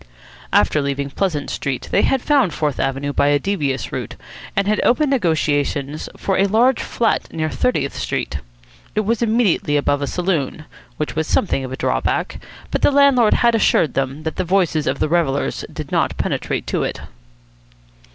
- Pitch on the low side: No, medium, 160 Hz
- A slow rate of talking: No, average, 175 wpm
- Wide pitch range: Yes, wide, 7.0 semitones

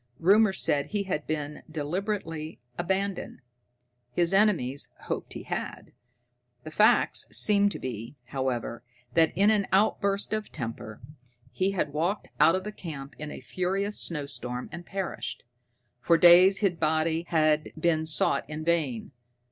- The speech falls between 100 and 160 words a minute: Yes, average, 140 wpm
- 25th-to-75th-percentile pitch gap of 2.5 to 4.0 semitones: No, average, 4.6 semitones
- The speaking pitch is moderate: Yes, medium, 165 Hz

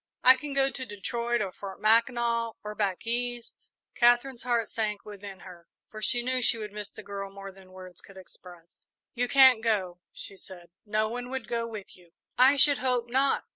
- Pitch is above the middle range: Yes, high, 225 Hz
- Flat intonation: No, average, 3.8 semitones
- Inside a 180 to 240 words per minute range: Yes, average, 195 wpm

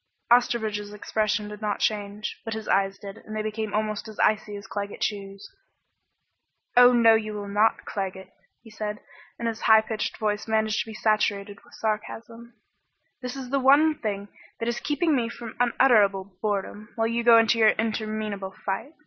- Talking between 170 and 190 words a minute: Yes, average, 175 wpm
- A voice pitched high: Yes, high, 215 Hz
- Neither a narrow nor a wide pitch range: No, narrow, 1.8 semitones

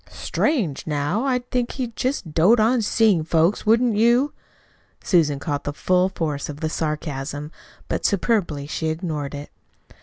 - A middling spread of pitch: No, wide, 7.3 semitones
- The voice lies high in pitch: No, medium, 170 Hz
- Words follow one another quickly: No, average, 150 wpm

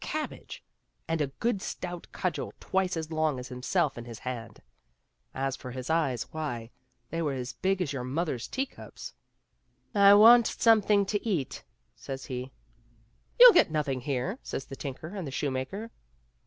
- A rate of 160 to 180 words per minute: Yes, average, 170 wpm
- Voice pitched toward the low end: No, medium, 150 Hz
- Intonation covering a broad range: Yes, wide, 6.9 semitones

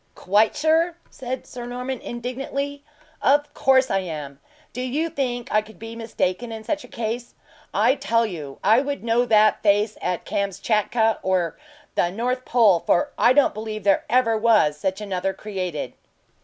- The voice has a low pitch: No, high, 225 Hz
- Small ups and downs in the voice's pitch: No, average, 4.1 semitones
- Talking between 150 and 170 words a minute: Yes, average, 165 wpm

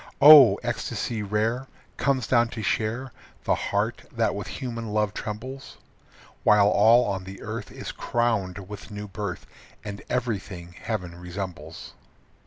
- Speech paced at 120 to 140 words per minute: Yes, slow, 135 wpm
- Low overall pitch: Yes, low, 105 Hz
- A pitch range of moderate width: Yes, average, 3.1 semitones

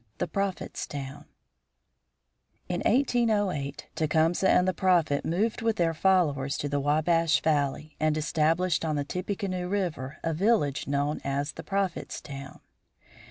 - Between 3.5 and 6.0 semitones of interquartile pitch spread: Yes, average, 4.5 semitones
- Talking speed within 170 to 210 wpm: No, slow, 135 wpm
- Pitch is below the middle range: No, medium, 160 Hz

